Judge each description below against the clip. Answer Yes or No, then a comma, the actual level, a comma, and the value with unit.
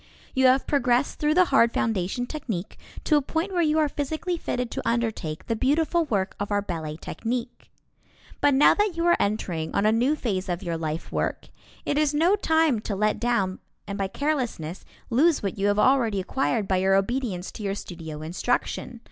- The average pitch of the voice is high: Yes, high, 235 Hz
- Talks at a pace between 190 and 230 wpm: Yes, average, 195 wpm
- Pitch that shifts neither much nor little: No, wide, 7.1 semitones